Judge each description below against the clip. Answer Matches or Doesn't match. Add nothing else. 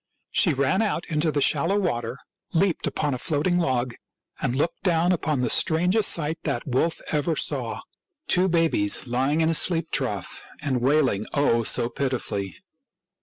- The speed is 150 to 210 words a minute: Matches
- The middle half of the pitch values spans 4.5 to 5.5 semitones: Matches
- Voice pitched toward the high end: Doesn't match